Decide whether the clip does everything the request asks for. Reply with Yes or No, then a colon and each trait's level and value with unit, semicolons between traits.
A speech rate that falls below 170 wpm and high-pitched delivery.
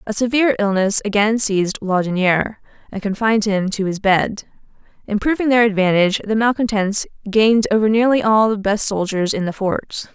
Yes: average, 160 wpm; high, 210 Hz